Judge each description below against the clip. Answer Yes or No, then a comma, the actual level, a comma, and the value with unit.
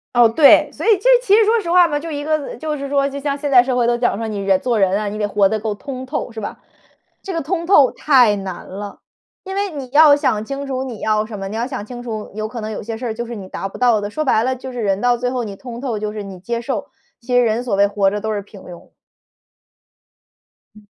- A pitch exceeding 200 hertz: Yes, high, 240 Hz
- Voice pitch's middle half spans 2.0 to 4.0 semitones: No, average, 4.8 semitones